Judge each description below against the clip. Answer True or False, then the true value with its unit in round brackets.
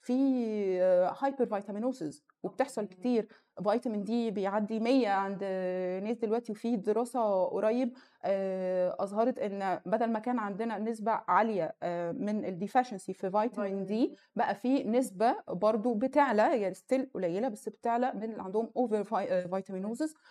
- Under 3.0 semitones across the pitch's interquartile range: False (3.9 semitones)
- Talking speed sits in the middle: True (125 wpm)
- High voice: True (220 Hz)